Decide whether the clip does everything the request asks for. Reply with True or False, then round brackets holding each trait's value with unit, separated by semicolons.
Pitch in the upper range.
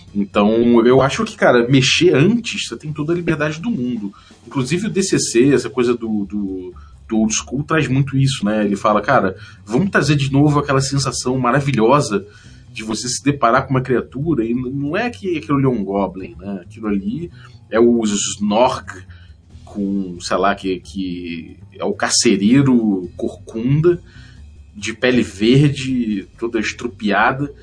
False (115 Hz)